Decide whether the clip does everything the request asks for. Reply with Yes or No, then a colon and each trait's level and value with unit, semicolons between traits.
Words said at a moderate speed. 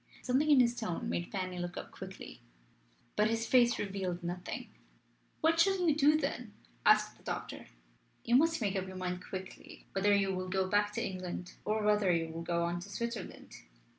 Yes: average, 190 wpm